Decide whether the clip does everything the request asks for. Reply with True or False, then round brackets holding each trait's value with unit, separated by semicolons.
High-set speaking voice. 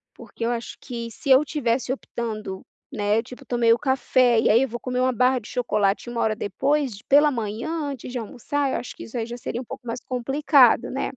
True (245 Hz)